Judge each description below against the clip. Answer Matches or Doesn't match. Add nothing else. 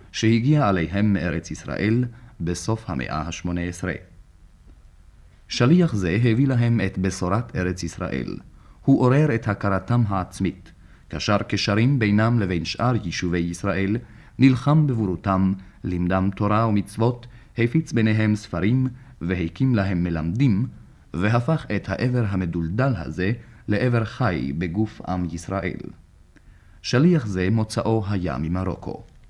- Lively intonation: Doesn't match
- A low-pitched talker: Matches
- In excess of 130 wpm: Doesn't match